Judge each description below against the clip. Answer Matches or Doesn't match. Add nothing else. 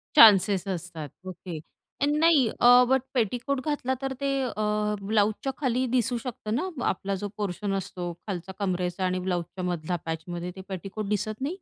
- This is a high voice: Matches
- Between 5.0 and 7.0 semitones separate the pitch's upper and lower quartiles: Matches